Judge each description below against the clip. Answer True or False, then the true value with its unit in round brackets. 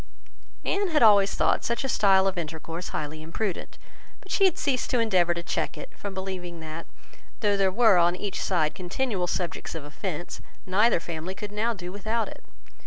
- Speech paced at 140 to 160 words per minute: False (185 wpm)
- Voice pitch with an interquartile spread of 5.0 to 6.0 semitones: False (3.9 semitones)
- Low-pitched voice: False (190 Hz)